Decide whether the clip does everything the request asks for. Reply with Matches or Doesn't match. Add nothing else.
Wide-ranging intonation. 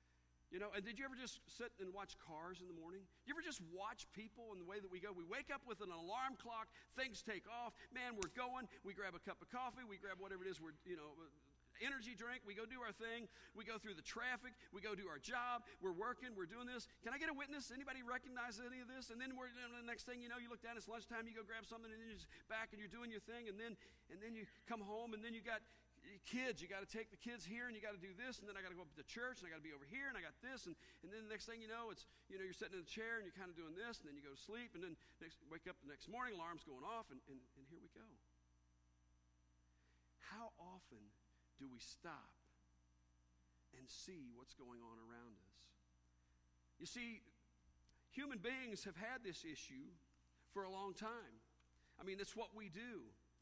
Matches